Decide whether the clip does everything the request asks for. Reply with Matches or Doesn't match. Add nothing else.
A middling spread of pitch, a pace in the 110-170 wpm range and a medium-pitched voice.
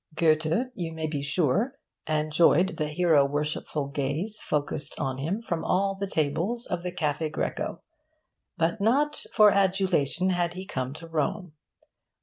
Matches